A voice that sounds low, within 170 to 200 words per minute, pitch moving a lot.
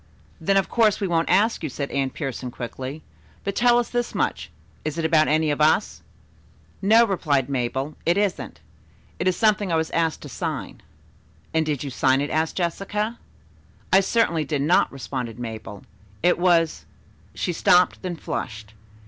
No: medium, 160 Hz; average, 175 wpm; wide, 5.7 semitones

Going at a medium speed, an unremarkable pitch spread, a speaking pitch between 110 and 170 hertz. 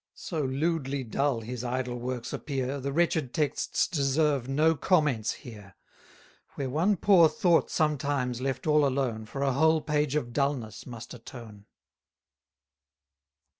No: slow, 130 wpm; average, 3.5 semitones; low, 135 Hz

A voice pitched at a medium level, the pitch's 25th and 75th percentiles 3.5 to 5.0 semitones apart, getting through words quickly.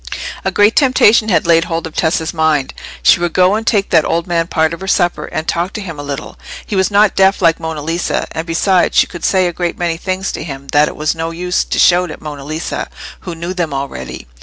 No: medium, 170 Hz; average, 2.8 semitones; fast, 245 wpm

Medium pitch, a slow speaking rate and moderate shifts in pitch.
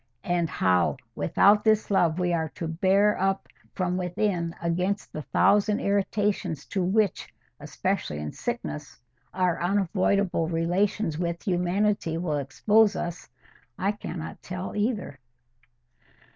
Yes: medium, 180 Hz; slow, 120 wpm; average, 3.4 semitones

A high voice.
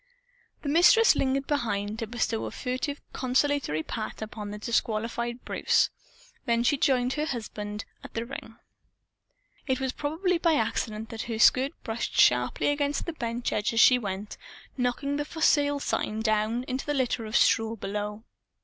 Yes: high, 240 Hz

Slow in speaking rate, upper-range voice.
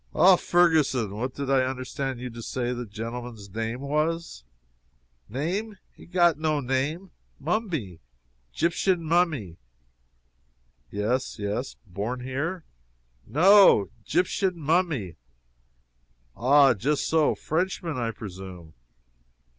No: slow, 105 wpm; low, 135 Hz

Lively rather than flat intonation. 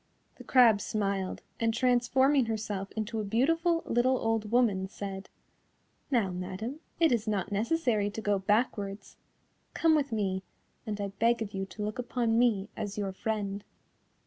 No: average, 3.3 semitones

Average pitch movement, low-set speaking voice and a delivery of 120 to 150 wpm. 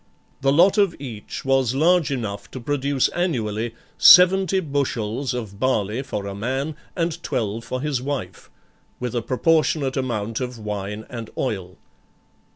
Yes: average, 4.7 semitones; low, 130 Hz; average, 145 wpm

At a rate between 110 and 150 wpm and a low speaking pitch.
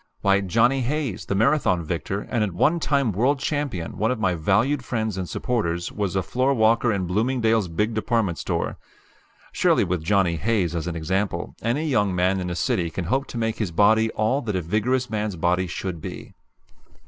No: average, 195 wpm; low, 105 Hz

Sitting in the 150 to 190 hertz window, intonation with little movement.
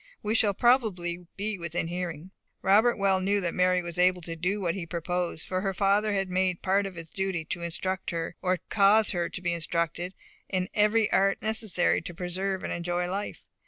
Yes: medium, 185 Hz; narrow, 2.3 semitones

